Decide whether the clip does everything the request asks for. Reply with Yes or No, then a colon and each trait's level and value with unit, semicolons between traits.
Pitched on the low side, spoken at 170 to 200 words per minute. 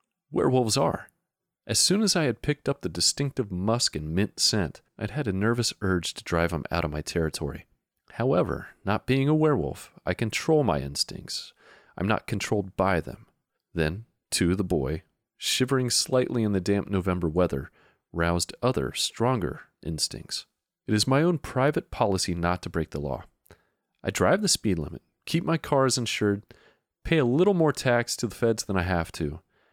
Yes: low, 105 Hz; average, 180 wpm